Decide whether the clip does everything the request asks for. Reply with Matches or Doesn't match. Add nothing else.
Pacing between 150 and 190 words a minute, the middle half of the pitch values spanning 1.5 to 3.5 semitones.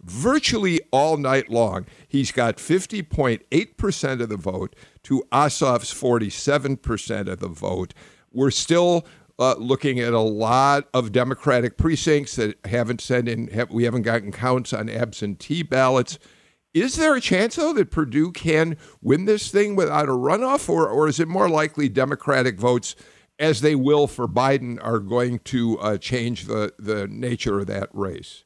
Doesn't match